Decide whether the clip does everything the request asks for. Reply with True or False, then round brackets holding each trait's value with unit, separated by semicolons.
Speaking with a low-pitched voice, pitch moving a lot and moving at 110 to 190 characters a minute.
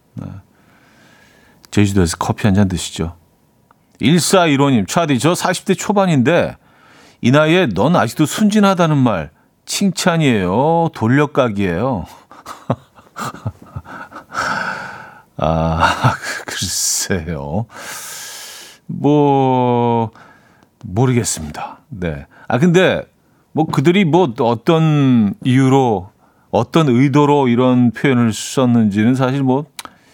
True (130 Hz; 6.2 semitones; 185 characters per minute)